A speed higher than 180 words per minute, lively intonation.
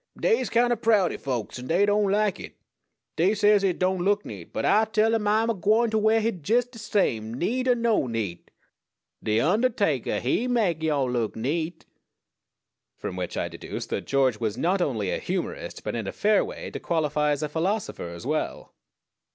Yes: average, 195 wpm; wide, 8.2 semitones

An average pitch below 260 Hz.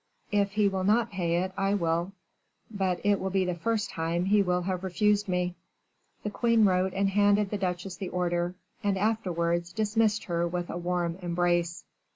Yes: medium, 185 Hz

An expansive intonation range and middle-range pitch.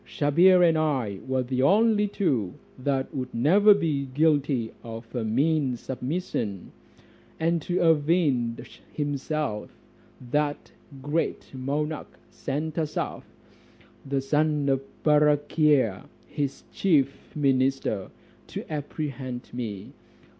No: average, 3.4 semitones; medium, 145 Hz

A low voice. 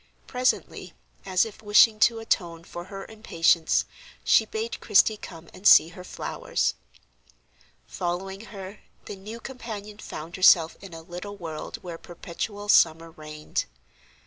No: high, 190 Hz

